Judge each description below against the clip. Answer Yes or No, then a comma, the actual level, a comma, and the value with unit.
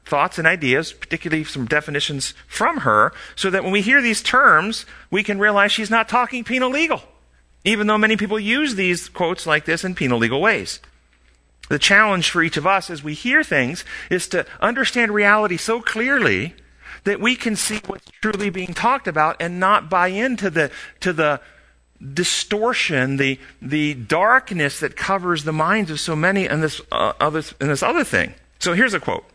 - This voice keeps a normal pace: Yes, average, 185 wpm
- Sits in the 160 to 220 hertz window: Yes, medium, 185 Hz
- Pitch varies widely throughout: Yes, wide, 5.7 semitones